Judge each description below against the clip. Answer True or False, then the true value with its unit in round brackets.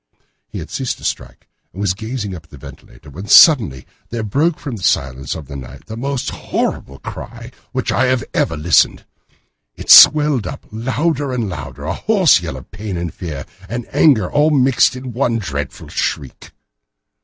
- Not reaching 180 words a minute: False (190 wpm)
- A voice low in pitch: True (110 Hz)